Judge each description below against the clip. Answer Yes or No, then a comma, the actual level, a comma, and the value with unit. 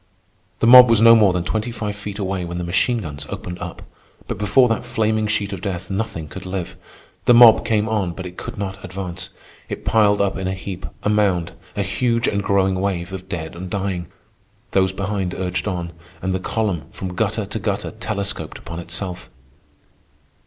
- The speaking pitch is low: Yes, low, 100 Hz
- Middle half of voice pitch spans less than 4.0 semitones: Yes, average, 2.8 semitones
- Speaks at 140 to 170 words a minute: No, average, 195 wpm